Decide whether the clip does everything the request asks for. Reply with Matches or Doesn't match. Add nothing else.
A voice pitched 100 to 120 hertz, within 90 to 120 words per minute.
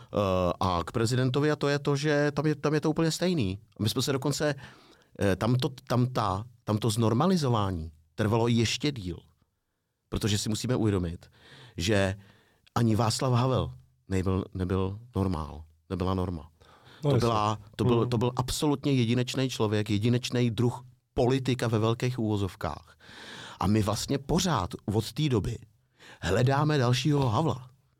Doesn't match